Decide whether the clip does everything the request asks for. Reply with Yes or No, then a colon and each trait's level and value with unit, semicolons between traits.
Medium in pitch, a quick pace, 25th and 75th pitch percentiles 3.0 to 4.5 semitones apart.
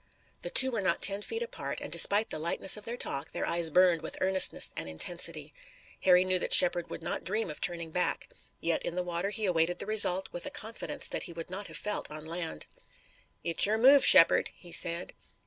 Yes: medium, 180 Hz; fast, 220 wpm; average, 3.7 semitones